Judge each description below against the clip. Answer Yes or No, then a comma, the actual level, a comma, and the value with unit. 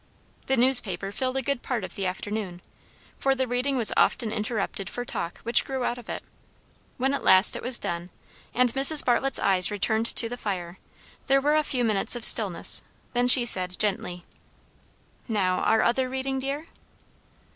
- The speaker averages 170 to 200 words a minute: Yes, average, 180 wpm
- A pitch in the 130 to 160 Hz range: No, high, 240 Hz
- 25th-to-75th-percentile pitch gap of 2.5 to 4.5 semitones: No, average, 5.0 semitones